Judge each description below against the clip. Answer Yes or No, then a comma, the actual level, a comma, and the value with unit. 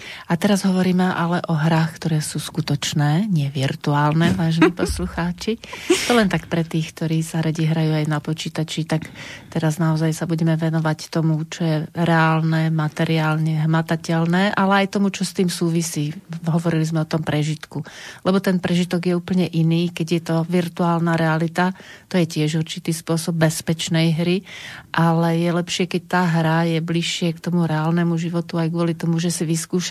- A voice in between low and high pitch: Yes, medium, 165 Hz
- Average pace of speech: No, fast, 170 wpm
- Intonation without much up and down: Yes, narrow, 1.6 semitones